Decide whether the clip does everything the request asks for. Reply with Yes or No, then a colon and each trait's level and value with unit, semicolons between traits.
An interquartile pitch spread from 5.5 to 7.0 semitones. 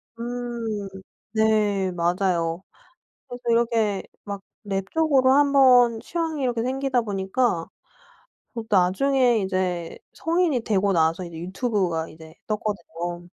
No: average, 5.1 semitones